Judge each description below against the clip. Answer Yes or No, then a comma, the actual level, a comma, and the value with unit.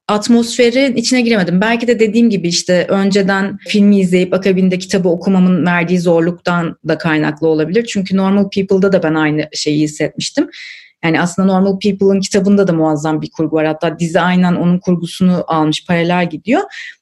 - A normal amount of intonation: Yes, average, 3.2 semitones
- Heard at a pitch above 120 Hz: Yes, medium, 185 Hz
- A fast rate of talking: Yes, fast, 160 wpm